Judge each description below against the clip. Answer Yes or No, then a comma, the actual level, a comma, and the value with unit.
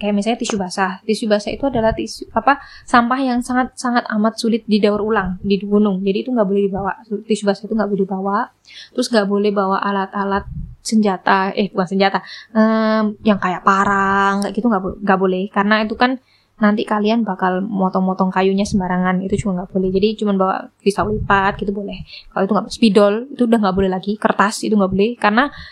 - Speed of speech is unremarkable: No, fast, 185 wpm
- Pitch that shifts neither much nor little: No, narrow, 2.2 semitones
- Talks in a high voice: Yes, high, 205 Hz